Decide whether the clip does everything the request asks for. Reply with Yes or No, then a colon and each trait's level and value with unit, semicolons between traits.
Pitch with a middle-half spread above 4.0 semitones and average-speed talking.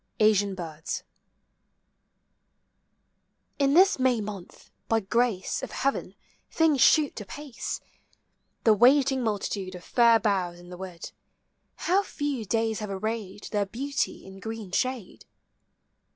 No: average, 5.1 semitones; slow, 125 wpm